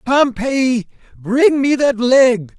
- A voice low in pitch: No, very high, 250 Hz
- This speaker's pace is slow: Yes, slow, 115 wpm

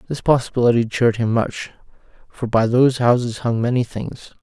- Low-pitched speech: Yes, low, 120 Hz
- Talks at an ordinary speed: Yes, average, 165 wpm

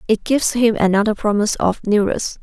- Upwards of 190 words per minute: No, average, 175 wpm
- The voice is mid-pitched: No, high, 215 Hz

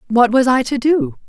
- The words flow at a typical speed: No, fast, 235 wpm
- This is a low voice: No, high, 245 Hz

